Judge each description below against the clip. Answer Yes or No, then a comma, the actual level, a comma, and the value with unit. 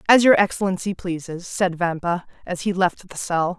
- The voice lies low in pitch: No, medium, 180 Hz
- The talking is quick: No, average, 185 wpm